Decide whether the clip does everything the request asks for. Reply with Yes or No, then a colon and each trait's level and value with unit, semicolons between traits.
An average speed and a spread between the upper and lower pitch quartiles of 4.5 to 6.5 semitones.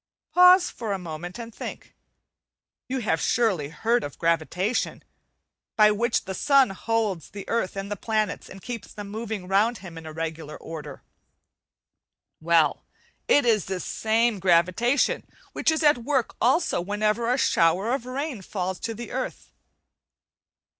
Yes: average, 150 wpm; average, 4.9 semitones